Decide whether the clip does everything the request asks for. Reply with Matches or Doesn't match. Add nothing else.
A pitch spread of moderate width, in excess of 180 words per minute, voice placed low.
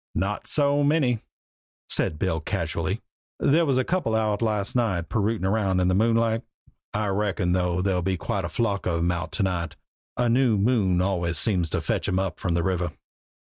Matches